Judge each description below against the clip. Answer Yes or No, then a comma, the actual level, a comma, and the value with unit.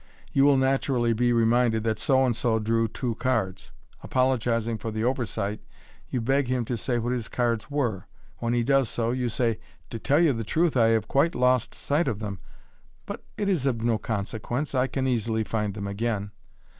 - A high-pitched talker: No, low, 120 Hz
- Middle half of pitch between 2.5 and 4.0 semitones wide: Yes, average, 2.8 semitones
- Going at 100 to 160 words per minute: No, fast, 205 wpm